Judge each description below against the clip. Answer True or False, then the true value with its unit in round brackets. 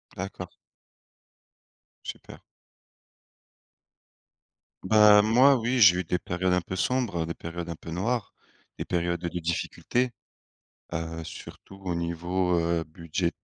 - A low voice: True (90 Hz)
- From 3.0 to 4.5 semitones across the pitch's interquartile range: True (3.5 semitones)